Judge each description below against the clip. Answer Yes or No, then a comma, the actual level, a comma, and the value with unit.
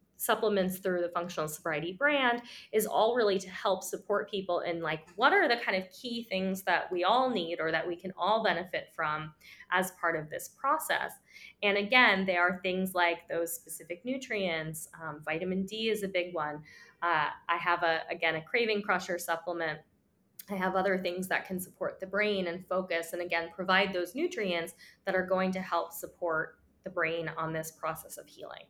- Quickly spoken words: No, average, 190 wpm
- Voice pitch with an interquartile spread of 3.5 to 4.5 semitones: No, average, 2.9 semitones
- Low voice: No, medium, 180 Hz